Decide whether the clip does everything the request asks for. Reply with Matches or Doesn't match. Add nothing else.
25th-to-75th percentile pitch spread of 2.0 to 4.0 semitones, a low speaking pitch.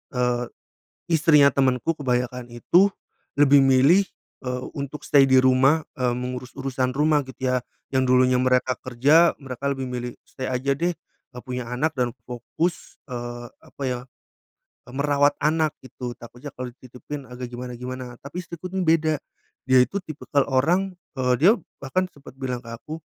Matches